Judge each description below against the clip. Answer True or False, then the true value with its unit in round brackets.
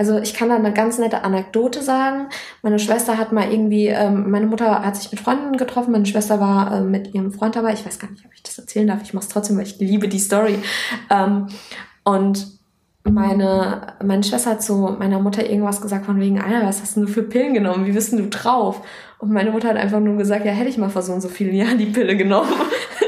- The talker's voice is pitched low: False (210 Hz)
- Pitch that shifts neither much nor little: False (2.1 semitones)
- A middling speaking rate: False (245 wpm)